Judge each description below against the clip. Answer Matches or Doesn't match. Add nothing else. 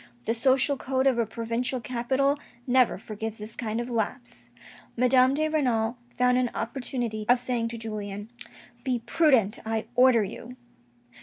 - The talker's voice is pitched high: Matches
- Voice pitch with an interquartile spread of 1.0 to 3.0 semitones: Matches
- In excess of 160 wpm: Doesn't match